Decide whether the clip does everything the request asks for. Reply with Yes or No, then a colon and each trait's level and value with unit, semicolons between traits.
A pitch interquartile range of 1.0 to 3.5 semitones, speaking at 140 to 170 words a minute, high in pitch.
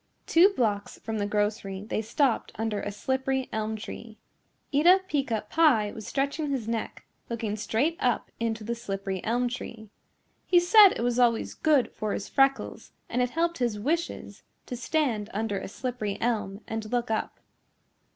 No: average, 4.0 semitones; average, 165 wpm; high, 230 Hz